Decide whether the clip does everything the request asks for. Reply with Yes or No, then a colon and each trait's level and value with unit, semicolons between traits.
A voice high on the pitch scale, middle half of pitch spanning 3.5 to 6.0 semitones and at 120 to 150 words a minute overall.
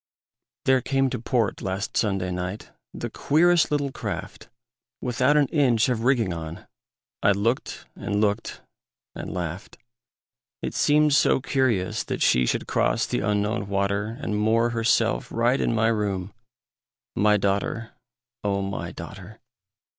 No: low, 110 Hz; average, 4.2 semitones; average, 140 wpm